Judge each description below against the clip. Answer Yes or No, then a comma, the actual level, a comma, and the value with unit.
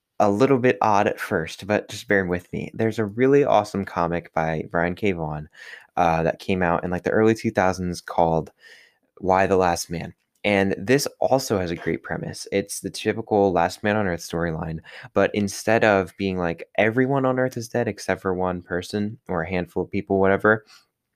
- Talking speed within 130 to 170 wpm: No, average, 195 wpm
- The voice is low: Yes, very low, 95 Hz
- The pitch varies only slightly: No, average, 3.8 semitones